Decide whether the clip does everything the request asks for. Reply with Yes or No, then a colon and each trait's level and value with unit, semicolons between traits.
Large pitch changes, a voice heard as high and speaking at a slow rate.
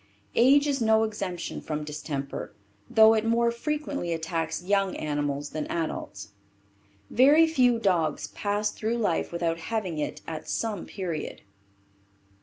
Yes: wide, 6.2 semitones; high, 195 Hz; slow, 130 wpm